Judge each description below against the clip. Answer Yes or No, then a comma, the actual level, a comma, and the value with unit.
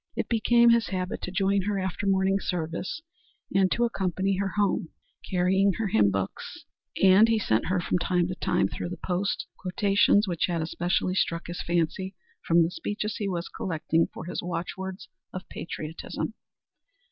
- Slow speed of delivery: No, average, 170 wpm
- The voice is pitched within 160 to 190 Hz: Yes, medium, 185 Hz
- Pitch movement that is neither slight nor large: No, narrow, 2.3 semitones